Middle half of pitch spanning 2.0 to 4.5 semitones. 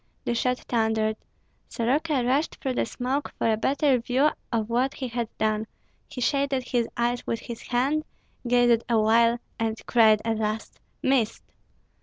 Yes: narrow, 2.5 semitones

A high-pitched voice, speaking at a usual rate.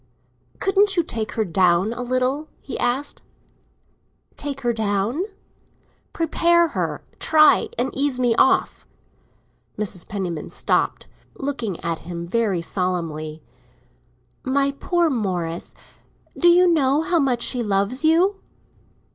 No: high, 245 Hz; slow, 115 wpm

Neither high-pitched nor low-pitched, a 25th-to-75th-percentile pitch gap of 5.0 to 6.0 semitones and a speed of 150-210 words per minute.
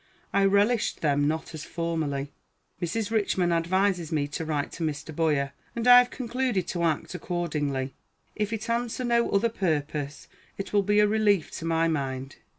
Yes: medium, 170 Hz; wide, 5.6 semitones; average, 170 wpm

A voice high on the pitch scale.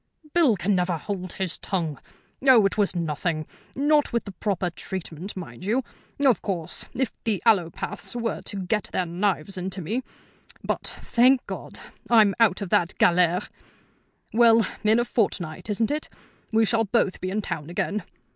Yes: high, 200 Hz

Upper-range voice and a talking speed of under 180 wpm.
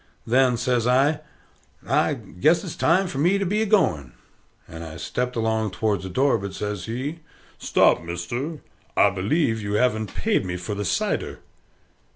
No: low, 115 Hz; average, 170 wpm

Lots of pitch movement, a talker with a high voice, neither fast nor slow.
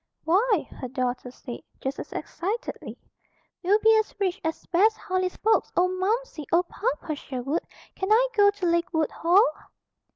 No: average, 4.7 semitones; very high, 365 Hz; average, 155 wpm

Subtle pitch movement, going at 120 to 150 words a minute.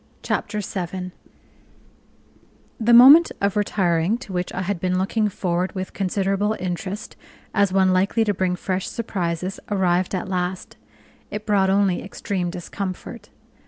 Yes: narrow, 2.0 semitones; slow, 135 wpm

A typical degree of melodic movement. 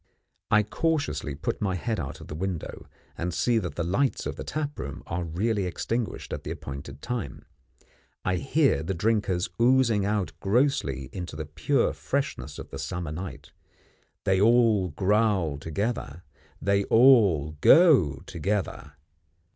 No: wide, 6.3 semitones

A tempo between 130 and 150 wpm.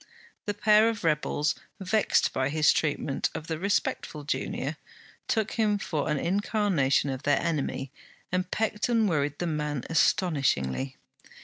Yes: average, 140 wpm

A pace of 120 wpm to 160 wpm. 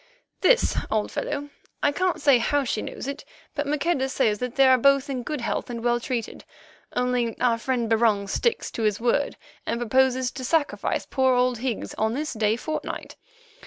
No: average, 185 wpm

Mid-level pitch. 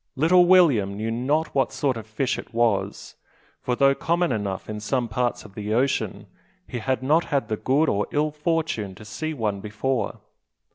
No: low, 125 Hz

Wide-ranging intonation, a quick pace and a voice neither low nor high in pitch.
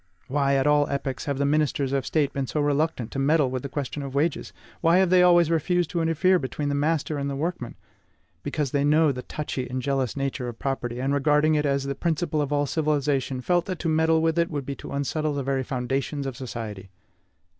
No: narrow, 2.6 semitones; fast, 225 wpm; medium, 145 Hz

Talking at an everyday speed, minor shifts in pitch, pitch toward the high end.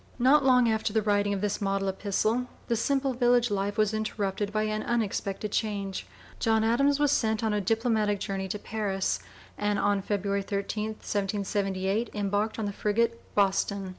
Yes: average, 165 wpm; narrow, 2.1 semitones; high, 210 Hz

